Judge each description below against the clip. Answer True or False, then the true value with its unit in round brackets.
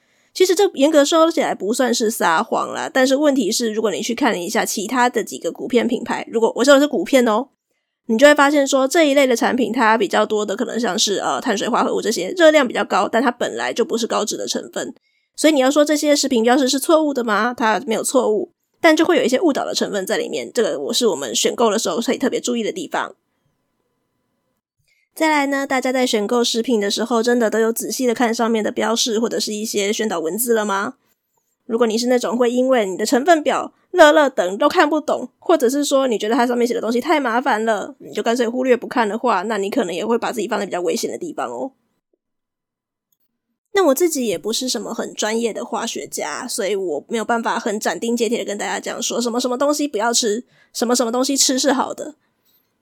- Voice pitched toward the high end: True (240 Hz)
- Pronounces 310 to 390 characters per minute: True (345 characters per minute)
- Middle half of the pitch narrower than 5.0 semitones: True (4.1 semitones)